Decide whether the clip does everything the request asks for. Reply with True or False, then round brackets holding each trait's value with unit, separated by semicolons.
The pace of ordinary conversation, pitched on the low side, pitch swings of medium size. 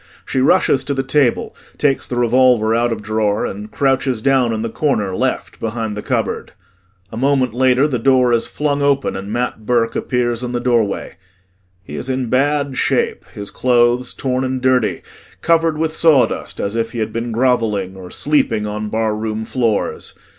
True (175 wpm; 120 Hz; 3.2 semitones)